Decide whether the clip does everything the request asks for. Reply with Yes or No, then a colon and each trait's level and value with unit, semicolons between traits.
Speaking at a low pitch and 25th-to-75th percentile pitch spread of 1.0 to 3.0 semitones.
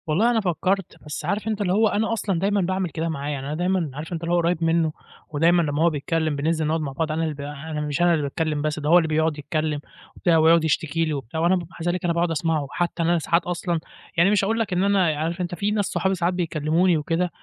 No: medium, 165 Hz; narrow, 2.6 semitones